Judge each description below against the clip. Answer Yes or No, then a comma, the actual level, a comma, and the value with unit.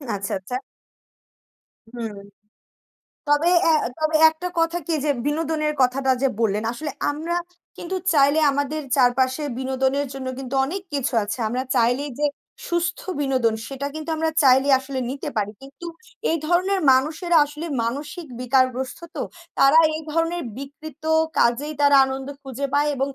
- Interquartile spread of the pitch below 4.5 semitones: Yes, average, 3.2 semitones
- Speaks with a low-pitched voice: No, very high, 280 Hz